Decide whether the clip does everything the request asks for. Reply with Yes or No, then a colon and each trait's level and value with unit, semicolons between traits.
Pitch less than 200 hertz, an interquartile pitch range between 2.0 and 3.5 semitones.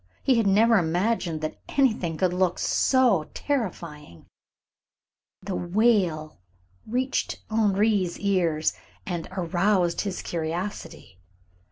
No: medium, 185 Hz; average, 4.5 semitones